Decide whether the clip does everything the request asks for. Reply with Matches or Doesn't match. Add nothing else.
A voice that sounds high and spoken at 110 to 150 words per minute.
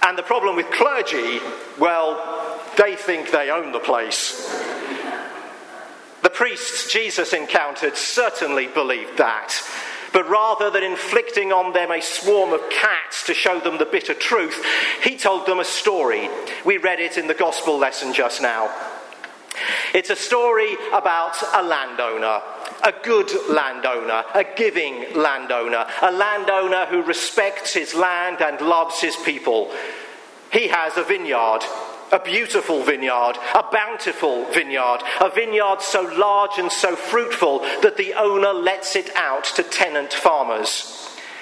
Matches